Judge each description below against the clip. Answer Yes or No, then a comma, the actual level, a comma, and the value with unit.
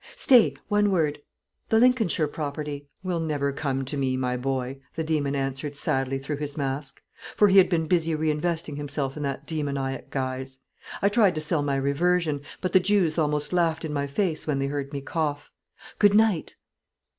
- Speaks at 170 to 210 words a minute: Yes, average, 190 wpm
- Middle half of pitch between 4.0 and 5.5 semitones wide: No, average, 3.5 semitones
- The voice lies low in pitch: No, medium, 150 Hz